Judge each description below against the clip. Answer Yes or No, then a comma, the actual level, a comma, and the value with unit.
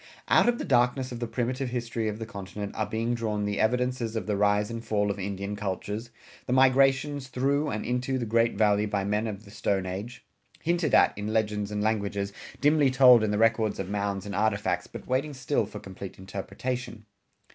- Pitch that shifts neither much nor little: Yes, average, 3.6 semitones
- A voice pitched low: Yes, low, 110 Hz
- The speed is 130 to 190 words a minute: No, average, 200 wpm